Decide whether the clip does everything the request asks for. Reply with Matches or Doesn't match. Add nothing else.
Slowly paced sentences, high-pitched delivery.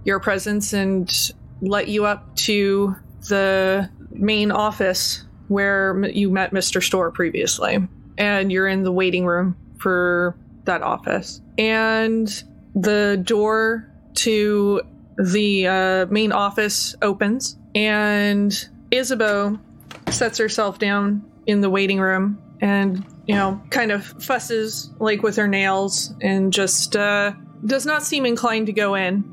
Matches